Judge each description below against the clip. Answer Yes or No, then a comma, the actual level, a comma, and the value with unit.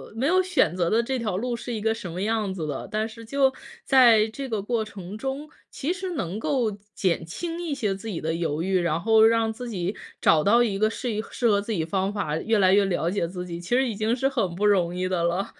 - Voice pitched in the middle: No, high, 215 Hz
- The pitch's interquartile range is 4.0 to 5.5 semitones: Yes, average, 4.6 semitones